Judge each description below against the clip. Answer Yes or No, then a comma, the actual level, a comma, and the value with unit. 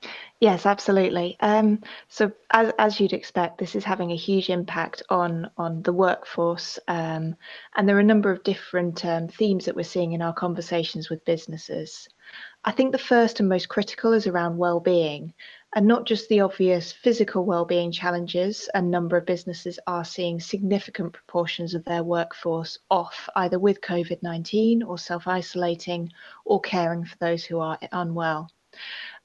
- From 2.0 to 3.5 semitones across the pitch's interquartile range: Yes, average, 2.8 semitones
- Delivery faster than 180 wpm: No, average, 160 wpm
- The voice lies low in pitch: No, medium, 180 Hz